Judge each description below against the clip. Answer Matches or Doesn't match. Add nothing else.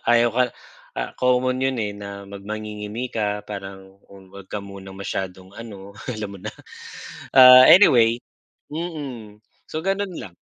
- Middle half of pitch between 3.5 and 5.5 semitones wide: Matches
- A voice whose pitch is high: Doesn't match